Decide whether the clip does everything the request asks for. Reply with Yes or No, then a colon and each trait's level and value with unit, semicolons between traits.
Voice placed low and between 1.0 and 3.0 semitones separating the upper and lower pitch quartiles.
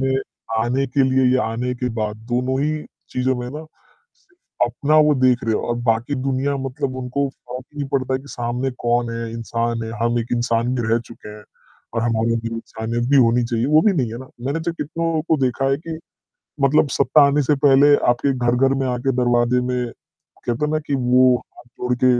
Yes: low, 125 Hz; average, 2.7 semitones